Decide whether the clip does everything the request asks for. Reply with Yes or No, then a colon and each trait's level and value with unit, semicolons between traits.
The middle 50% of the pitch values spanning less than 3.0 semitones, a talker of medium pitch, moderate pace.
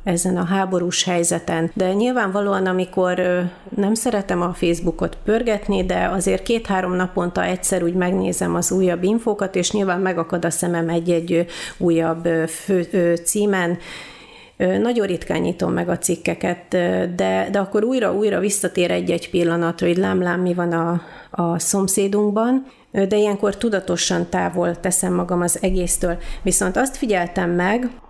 Yes: narrow, 2.6 semitones; medium, 180 Hz; average, 135 wpm